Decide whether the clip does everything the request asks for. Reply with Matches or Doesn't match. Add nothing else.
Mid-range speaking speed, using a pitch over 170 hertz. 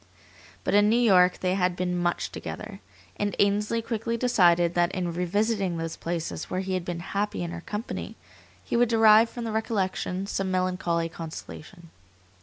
Matches